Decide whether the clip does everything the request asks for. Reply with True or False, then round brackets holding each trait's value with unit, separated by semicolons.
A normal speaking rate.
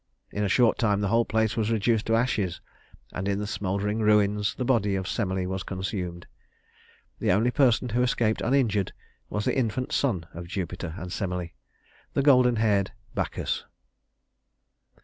True (160 wpm)